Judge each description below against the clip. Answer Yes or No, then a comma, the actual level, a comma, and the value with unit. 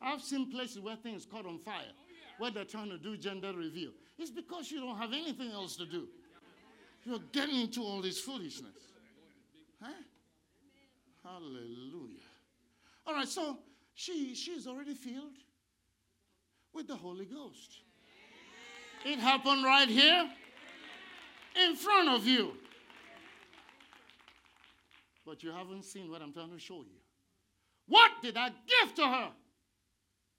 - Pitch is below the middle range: No, very high, 255 Hz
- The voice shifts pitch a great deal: Yes, wide, 6.9 semitones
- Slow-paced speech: Yes, slow, 130 wpm